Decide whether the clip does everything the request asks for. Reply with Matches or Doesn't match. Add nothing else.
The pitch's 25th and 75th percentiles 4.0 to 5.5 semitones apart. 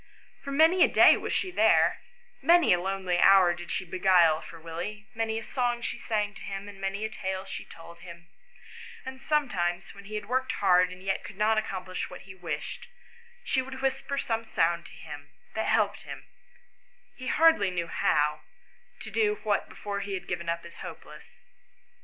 Matches